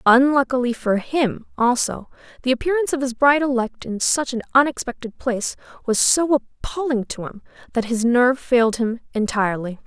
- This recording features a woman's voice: Yes, female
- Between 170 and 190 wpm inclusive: No, average, 160 wpm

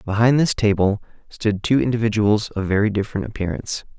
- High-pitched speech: No, low, 105 Hz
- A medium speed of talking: Yes, average, 150 wpm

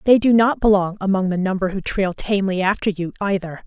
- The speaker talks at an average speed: No, fast, 215 wpm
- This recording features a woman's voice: Yes, female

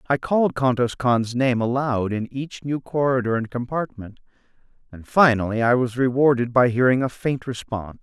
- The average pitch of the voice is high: No, low, 125 Hz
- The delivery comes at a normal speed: Yes, average, 165 wpm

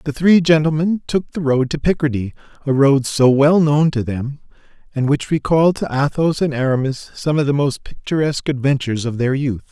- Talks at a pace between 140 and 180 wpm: No, average, 190 wpm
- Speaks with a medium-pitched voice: Yes, medium, 145 Hz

